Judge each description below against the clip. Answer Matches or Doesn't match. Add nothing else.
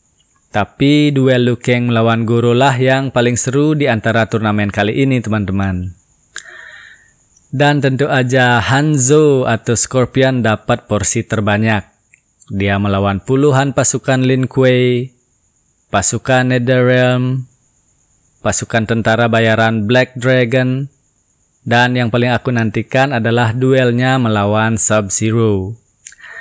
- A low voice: Matches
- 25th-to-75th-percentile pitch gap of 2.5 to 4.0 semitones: Matches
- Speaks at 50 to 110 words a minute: Matches